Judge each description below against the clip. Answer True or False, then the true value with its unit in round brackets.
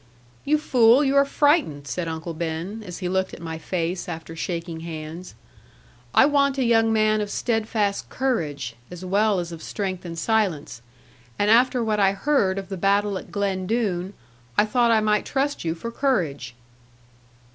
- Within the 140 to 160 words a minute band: False (175 wpm)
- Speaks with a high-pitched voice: True (200 Hz)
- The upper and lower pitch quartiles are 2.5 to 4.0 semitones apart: False (5.1 semitones)